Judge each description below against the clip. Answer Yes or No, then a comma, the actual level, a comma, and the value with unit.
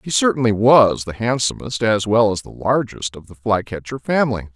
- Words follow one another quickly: No, average, 185 wpm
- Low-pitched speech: Yes, low, 110 Hz